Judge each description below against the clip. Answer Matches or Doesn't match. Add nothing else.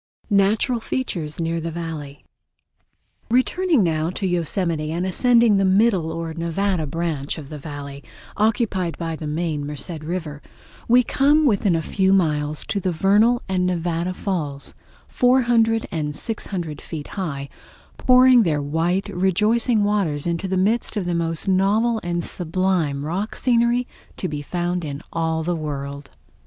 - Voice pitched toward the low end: Doesn't match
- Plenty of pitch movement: Doesn't match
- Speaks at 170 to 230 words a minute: Doesn't match